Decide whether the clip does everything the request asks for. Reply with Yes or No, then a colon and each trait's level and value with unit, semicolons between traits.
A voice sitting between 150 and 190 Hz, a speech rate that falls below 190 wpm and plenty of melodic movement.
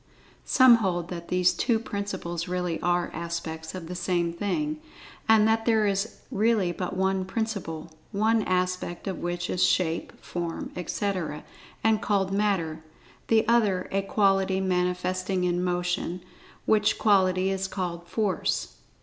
No: medium, 185 Hz; average, 140 wpm; average, 2.7 semitones